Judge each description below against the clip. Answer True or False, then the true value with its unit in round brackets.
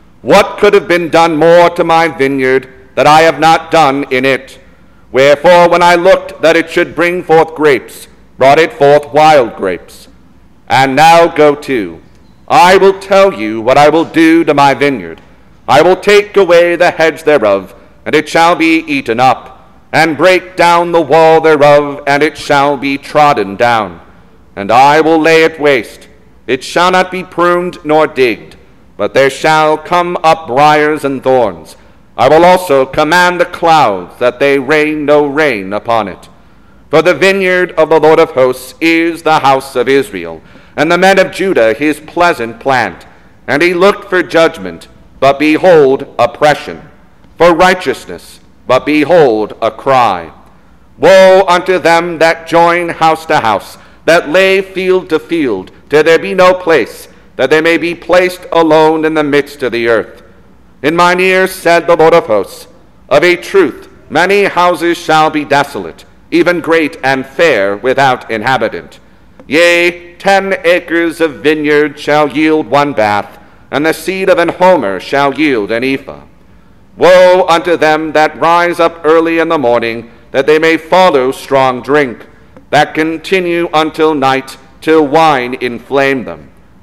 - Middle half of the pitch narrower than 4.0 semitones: True (3.6 semitones)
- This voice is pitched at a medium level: True (160 Hz)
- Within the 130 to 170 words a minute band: True (160 wpm)